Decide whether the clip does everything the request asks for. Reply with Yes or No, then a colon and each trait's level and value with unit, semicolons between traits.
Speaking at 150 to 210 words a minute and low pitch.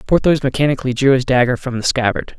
Yes: average, 200 wpm; low, 130 Hz